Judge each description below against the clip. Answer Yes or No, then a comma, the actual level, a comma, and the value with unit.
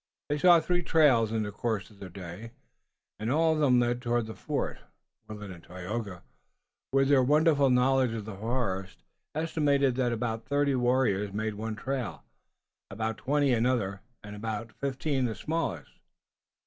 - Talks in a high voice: No, low, 120 Hz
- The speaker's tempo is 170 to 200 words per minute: No, average, 155 wpm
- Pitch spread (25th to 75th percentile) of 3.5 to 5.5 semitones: Yes, average, 4.6 semitones